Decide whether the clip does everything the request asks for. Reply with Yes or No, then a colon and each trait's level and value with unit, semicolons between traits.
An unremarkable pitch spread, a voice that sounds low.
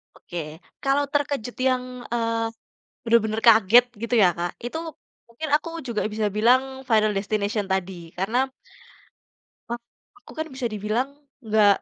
No: average, 3.3 semitones; high, 225 Hz